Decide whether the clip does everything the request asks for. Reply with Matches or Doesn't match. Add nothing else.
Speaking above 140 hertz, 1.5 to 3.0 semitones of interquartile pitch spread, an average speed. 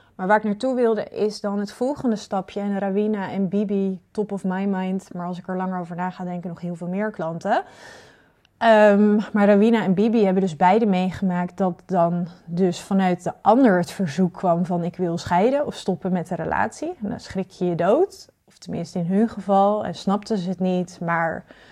Doesn't match